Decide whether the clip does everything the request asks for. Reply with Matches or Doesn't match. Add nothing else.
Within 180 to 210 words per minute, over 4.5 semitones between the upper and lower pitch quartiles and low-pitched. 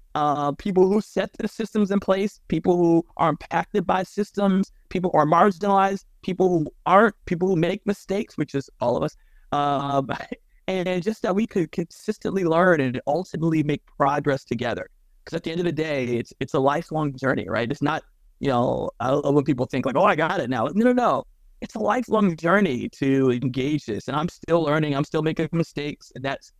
Doesn't match